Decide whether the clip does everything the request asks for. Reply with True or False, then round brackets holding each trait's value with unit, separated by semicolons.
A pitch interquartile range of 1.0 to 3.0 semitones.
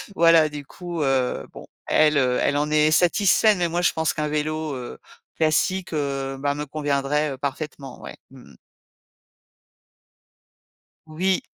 True (2.6 semitones)